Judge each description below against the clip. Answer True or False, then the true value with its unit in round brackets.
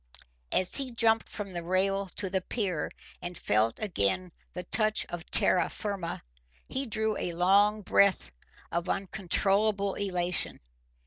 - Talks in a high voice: True (195 Hz)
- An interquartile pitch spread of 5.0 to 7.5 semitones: False (2.9 semitones)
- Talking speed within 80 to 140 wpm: True (135 wpm)